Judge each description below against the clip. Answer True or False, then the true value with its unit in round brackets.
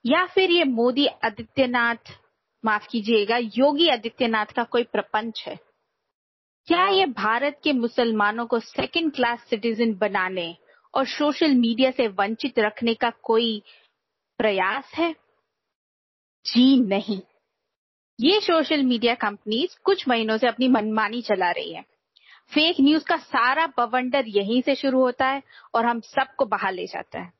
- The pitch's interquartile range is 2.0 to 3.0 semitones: False (4.5 semitones)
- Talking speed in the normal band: True (140 wpm)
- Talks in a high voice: True (245 Hz)